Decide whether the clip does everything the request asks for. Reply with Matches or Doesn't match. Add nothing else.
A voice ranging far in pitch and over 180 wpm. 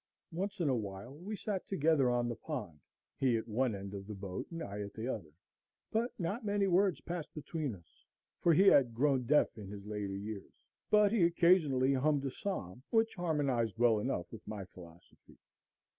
Matches